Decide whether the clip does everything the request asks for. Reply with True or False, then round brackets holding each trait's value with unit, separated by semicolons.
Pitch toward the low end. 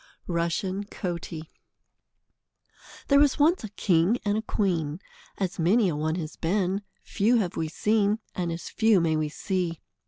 False (185 Hz)